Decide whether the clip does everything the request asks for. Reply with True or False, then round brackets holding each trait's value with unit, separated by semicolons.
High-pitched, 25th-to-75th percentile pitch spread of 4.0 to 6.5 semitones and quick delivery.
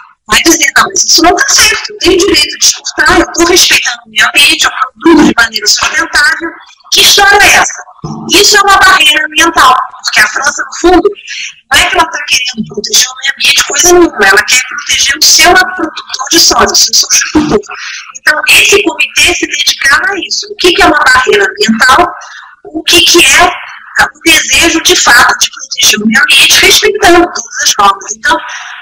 True (335 Hz; 4.3 semitones; 195 wpm)